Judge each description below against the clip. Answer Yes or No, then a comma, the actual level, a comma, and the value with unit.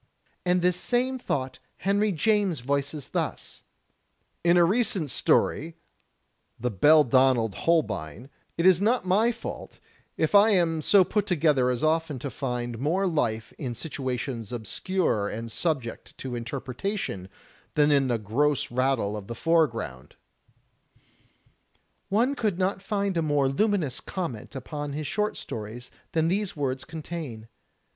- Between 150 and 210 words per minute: No, slow, 135 wpm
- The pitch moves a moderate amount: No, wide, 6.9 semitones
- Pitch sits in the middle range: Yes, medium, 150 Hz